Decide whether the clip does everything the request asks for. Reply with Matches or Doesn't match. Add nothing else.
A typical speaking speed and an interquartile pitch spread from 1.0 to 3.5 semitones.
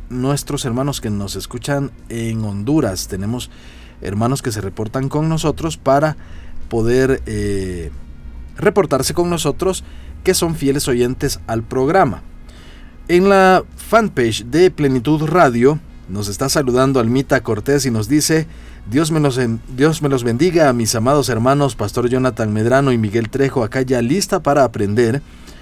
Doesn't match